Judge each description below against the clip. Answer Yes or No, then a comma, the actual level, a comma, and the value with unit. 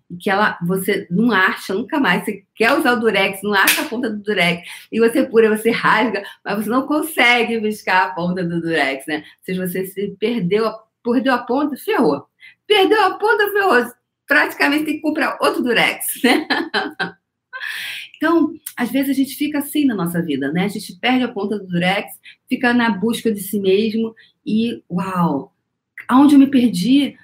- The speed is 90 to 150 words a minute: No, average, 180 wpm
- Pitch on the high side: Yes, high, 225 Hz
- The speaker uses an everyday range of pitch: No, wide, 5.8 semitones